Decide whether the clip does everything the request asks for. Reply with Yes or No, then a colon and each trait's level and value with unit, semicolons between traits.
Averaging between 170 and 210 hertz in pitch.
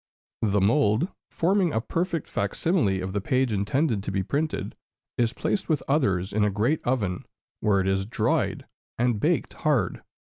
No: low, 110 Hz